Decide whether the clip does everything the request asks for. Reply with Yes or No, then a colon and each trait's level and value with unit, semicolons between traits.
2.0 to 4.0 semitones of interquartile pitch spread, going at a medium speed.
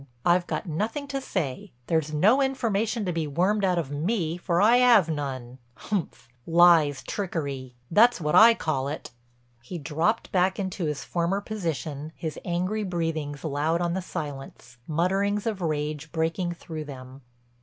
No: average, 4.8 semitones; average, 150 wpm